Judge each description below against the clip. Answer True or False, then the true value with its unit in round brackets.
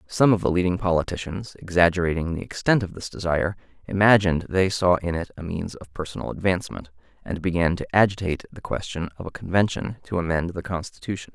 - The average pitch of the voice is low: True (90 Hz)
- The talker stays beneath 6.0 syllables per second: False (6.3 syllables/s)